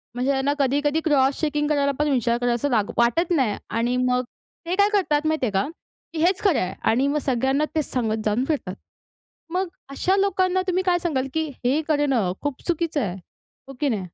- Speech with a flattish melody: No, average, 4.4 semitones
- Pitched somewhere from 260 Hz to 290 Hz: Yes, very high, 280 Hz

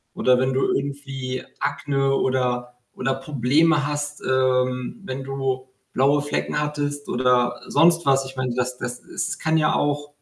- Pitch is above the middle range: No, low, 135 Hz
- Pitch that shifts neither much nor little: No, narrow, 2.2 semitones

